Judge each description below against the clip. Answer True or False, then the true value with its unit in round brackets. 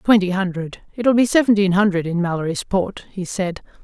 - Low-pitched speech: False (190 Hz)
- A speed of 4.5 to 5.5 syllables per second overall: True (5.3 syllables/s)